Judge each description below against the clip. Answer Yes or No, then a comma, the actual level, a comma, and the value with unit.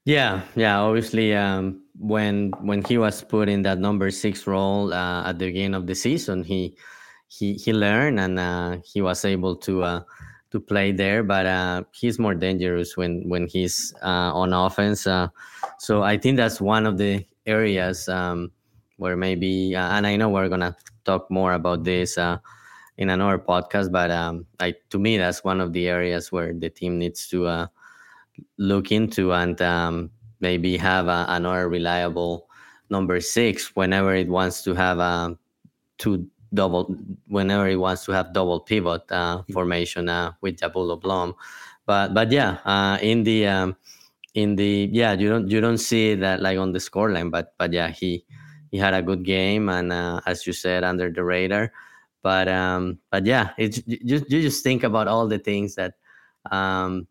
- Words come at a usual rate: Yes, average, 180 wpm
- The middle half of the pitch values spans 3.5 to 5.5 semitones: No, narrow, 2.4 semitones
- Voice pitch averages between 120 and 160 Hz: No, very low, 95 Hz